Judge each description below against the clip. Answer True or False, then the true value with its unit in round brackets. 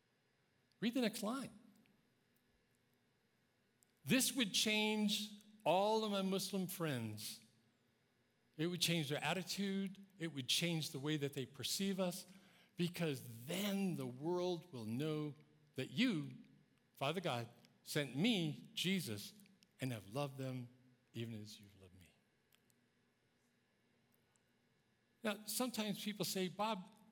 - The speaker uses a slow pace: True (115 wpm)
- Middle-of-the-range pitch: True (170 Hz)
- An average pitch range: False (8.0 semitones)